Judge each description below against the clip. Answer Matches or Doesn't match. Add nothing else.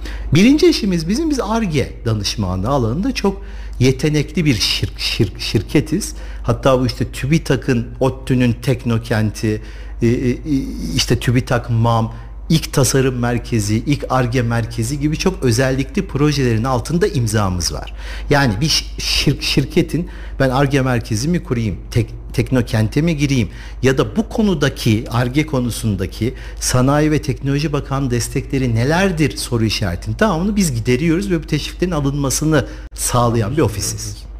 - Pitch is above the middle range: Doesn't match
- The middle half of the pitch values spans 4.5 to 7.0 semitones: Matches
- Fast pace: Doesn't match